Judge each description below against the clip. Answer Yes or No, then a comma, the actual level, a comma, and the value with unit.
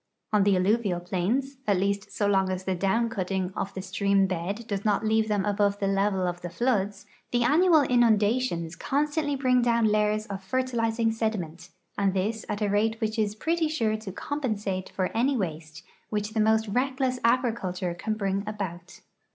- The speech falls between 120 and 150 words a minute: No, average, 185 wpm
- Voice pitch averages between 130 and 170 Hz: No, high, 210 Hz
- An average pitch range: Yes, average, 3.4 semitones